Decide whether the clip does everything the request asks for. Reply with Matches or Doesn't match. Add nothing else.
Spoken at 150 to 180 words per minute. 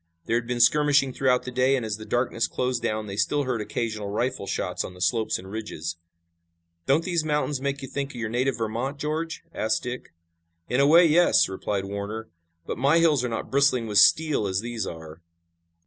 Doesn't match